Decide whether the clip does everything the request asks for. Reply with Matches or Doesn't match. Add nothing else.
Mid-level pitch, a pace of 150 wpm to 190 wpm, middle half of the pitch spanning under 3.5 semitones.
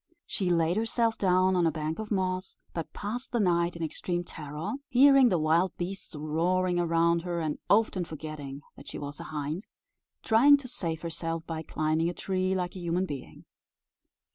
Matches